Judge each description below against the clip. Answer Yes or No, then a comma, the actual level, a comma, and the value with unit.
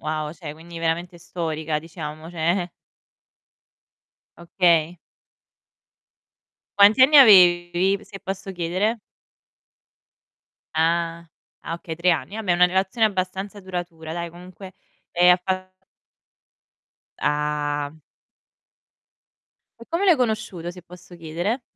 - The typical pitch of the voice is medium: Yes, medium, 175 Hz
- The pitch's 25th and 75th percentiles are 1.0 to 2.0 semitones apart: No, narrow, 2.6 semitones